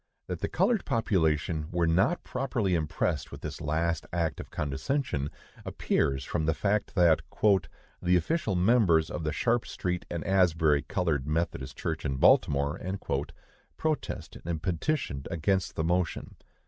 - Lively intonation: No, average, 4.0 semitones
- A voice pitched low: Yes, very low, 85 Hz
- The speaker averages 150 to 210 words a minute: No, average, 140 wpm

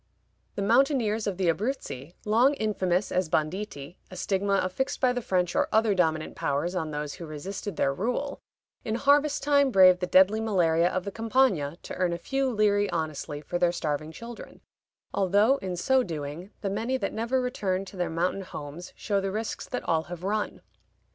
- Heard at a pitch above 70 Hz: Yes, high, 190 Hz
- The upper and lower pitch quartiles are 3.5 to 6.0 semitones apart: Yes, average, 4.7 semitones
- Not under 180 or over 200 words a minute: Yes, average, 185 wpm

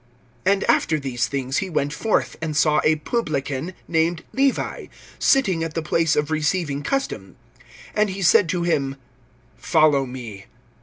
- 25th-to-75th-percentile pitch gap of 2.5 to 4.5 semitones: Yes, average, 4.2 semitones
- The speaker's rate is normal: Yes, average, 150 wpm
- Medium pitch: Yes, medium, 155 Hz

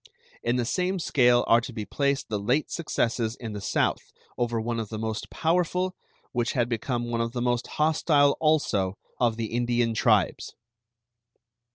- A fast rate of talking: No, average, 170 wpm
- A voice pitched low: Yes, low, 120 Hz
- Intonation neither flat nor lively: Yes, average, 3.7 semitones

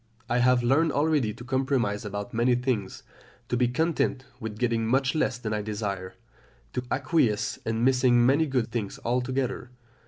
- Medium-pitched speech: No, low, 125 Hz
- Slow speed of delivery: No, average, 160 wpm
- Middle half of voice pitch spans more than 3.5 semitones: No, average, 3.0 semitones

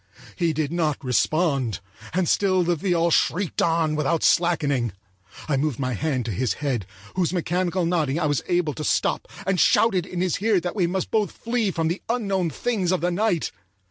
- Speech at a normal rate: Yes, average, 190 wpm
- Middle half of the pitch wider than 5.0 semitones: No, average, 3.7 semitones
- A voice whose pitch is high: No, medium, 170 Hz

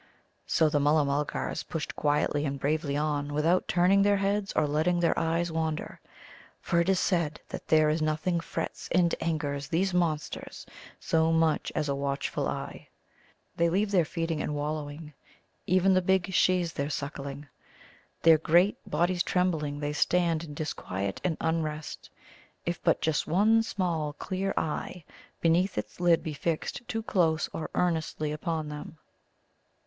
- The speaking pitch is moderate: Yes, medium, 160 Hz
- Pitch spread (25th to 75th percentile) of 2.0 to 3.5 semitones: Yes, average, 2.9 semitones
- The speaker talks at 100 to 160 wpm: Yes, average, 155 wpm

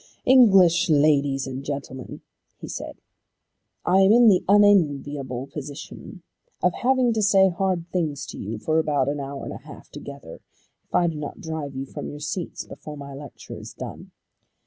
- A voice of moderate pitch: Yes, medium, 150 Hz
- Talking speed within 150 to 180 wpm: Yes, average, 170 wpm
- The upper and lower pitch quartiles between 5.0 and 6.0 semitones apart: Yes, average, 5.3 semitones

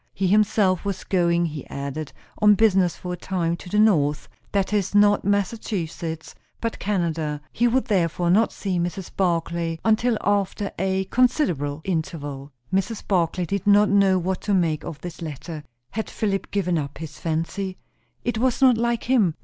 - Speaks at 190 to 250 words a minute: No, average, 165 wpm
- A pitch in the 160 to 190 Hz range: Yes, medium, 185 Hz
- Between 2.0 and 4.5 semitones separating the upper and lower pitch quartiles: Yes, average, 3.8 semitones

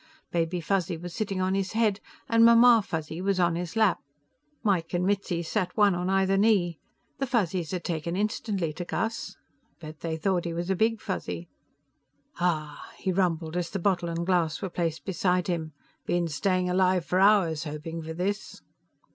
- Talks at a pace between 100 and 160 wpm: No, average, 180 wpm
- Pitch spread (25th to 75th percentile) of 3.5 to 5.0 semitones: No, average, 2.8 semitones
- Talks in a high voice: No, medium, 180 Hz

